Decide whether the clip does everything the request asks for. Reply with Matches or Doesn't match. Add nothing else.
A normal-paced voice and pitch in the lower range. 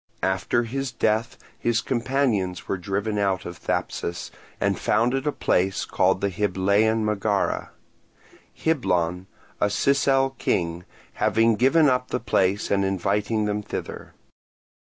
Doesn't match